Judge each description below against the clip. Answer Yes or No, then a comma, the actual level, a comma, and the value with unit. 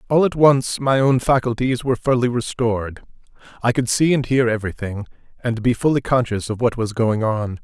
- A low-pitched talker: Yes, low, 120 Hz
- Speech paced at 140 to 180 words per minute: No, average, 190 wpm